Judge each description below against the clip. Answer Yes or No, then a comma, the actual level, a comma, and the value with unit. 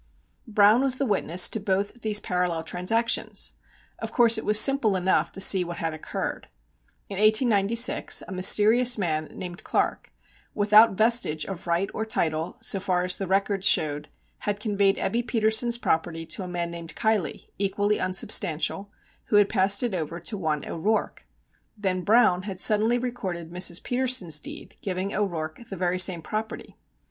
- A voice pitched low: No, high, 195 Hz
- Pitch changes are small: No, average, 3.6 semitones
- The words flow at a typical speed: Yes, average, 160 wpm